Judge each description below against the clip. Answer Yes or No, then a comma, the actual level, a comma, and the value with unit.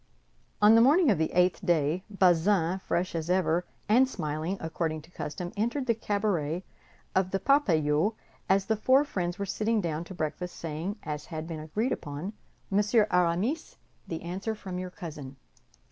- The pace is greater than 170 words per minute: No, average, 165 wpm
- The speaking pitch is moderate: Yes, medium, 180 Hz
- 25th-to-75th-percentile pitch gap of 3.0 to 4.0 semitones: No, average, 4.5 semitones